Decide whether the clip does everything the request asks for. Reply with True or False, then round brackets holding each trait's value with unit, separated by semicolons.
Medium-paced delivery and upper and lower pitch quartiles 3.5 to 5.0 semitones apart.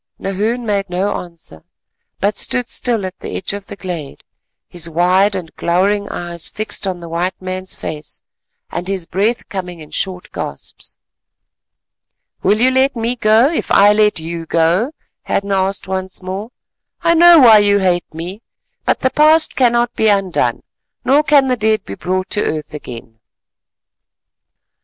True (160 wpm; 4.1 semitones)